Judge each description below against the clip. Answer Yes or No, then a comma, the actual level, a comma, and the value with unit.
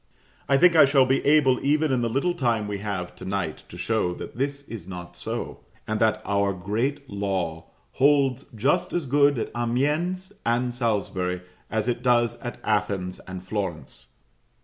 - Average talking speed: Yes, average, 170 wpm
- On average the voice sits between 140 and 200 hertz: No, low, 120 Hz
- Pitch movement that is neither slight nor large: No, wide, 5.8 semitones